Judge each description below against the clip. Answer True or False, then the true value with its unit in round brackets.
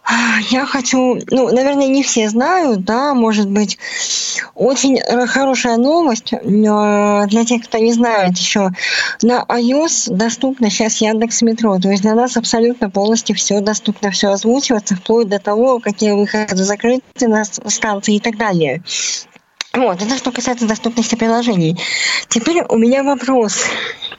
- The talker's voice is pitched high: True (230 Hz)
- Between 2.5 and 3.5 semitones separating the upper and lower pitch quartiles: True (3.1 semitones)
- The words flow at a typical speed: True (140 wpm)